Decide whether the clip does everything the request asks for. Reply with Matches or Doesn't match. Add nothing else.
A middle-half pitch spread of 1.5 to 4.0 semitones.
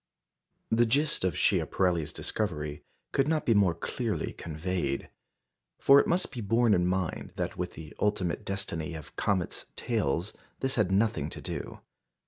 Doesn't match